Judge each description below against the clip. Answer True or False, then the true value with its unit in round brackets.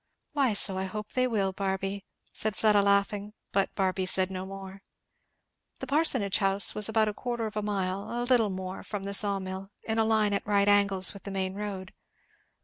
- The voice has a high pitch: True (200 Hz)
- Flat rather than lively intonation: True (1.9 semitones)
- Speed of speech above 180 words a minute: True (200 wpm)